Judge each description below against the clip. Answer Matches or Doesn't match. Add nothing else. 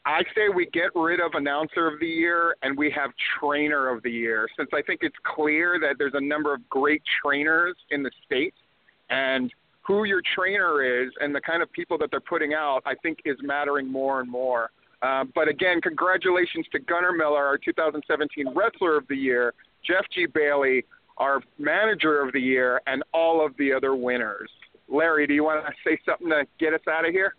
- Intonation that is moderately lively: Matches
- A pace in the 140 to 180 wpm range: Doesn't match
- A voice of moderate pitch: Matches